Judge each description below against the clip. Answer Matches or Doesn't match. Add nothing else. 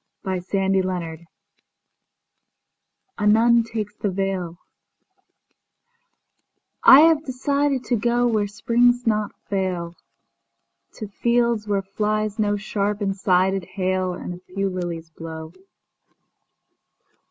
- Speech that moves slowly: Matches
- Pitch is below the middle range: Doesn't match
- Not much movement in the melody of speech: Doesn't match